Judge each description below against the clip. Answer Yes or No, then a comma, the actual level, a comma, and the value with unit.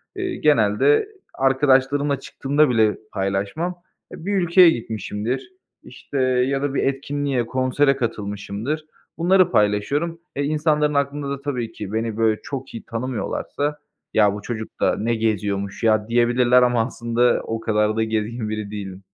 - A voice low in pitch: Yes, low, 125 Hz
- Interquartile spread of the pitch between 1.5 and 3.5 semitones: No, average, 4.8 semitones